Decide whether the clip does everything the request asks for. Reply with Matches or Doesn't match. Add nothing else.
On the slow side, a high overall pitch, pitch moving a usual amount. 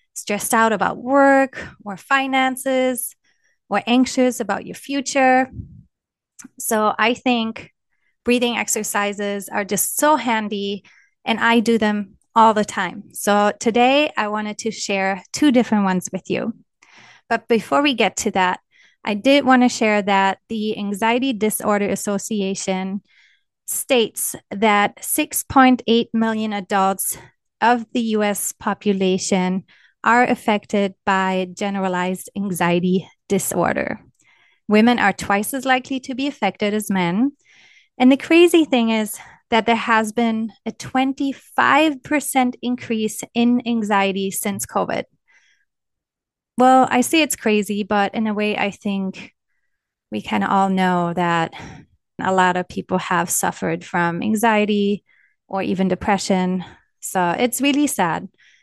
Matches